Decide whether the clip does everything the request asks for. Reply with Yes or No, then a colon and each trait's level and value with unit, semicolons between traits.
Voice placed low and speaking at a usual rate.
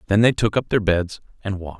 No: low, 100 Hz; fast, 270 wpm